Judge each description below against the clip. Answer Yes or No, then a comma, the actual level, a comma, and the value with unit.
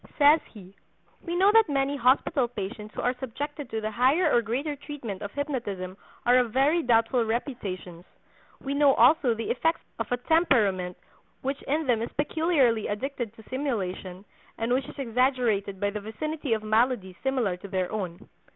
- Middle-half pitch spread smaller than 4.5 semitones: No, average, 5.1 semitones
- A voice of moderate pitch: No, high, 245 Hz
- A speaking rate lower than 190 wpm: Yes, average, 170 wpm